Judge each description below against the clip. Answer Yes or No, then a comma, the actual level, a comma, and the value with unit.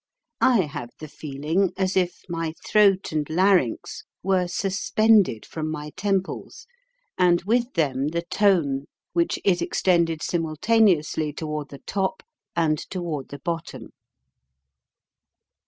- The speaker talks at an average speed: No, slow, 120 wpm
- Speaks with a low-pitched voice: No, medium, 170 Hz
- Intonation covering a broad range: No, average, 3.9 semitones